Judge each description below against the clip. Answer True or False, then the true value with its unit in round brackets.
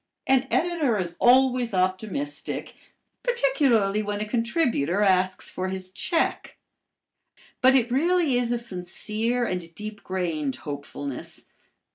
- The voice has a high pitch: True (215 Hz)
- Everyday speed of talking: False (115 wpm)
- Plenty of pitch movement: True (5.8 semitones)